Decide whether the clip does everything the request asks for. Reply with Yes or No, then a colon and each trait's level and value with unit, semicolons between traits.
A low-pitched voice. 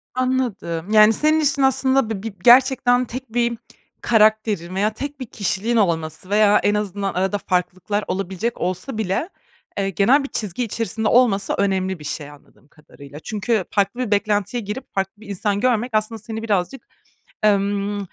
No: high, 210 Hz